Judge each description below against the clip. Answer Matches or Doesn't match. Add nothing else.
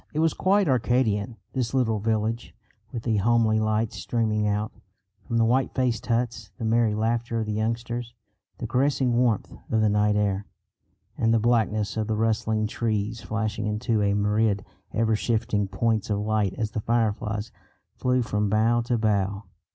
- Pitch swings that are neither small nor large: Doesn't match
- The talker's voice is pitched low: Matches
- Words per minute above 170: Doesn't match